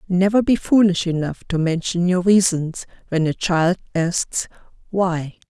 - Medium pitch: Yes, medium, 180 Hz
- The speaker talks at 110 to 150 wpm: Yes, average, 140 wpm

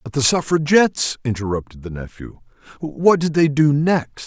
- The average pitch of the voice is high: No, medium, 140 Hz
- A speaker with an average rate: Yes, average, 155 wpm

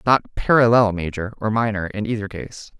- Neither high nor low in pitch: No, low, 105 Hz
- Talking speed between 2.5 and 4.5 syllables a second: No, 5.4 syllables/s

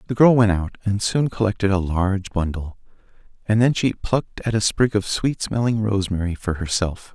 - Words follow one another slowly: No, average, 195 wpm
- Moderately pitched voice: No, low, 105 Hz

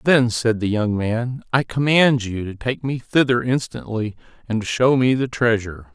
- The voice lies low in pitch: Yes, low, 120 Hz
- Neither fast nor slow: Yes, average, 190 wpm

